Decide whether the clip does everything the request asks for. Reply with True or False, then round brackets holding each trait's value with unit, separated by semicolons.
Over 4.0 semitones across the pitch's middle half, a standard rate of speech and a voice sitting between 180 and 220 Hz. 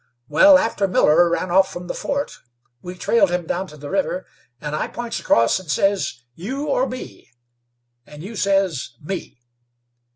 True (5.2 semitones; 165 wpm; 185 Hz)